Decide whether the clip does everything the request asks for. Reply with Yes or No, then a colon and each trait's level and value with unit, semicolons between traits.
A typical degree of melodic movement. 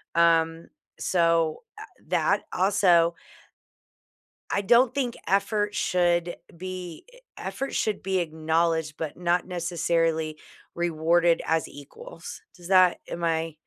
No: narrow, 2.2 semitones